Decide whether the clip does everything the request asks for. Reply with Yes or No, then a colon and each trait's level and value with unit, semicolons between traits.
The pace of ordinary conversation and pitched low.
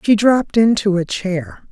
No: average, 175 wpm; high, 205 Hz